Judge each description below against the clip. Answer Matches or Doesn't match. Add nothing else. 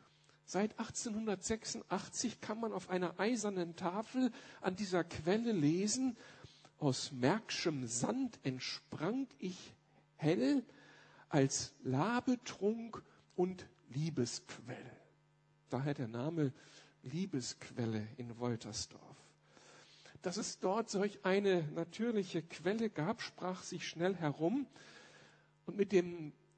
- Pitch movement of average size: Doesn't match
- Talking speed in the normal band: Doesn't match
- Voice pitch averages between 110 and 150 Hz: Doesn't match